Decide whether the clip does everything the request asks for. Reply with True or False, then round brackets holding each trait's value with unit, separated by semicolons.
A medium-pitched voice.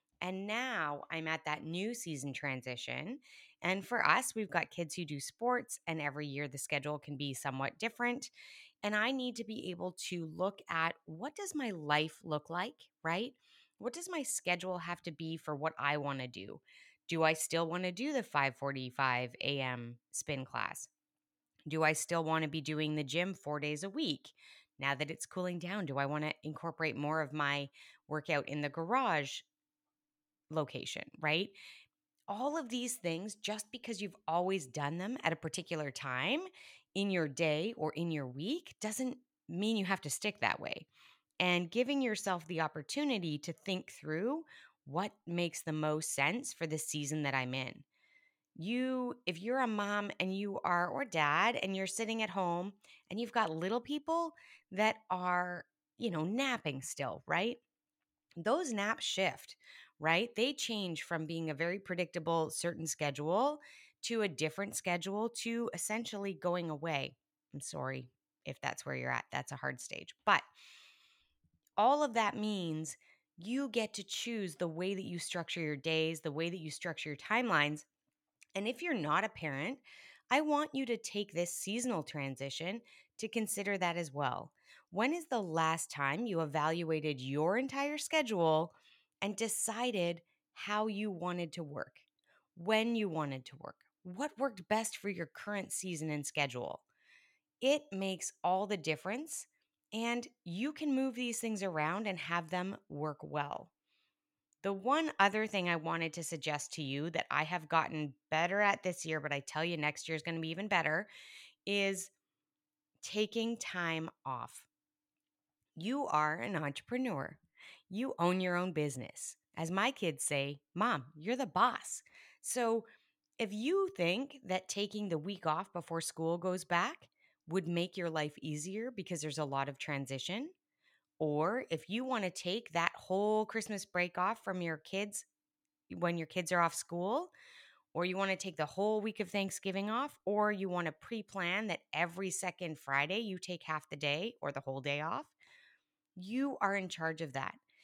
True (180 Hz)